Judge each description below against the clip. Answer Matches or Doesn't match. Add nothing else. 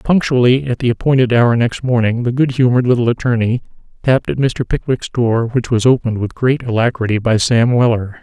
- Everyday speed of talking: Matches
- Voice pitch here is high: Doesn't match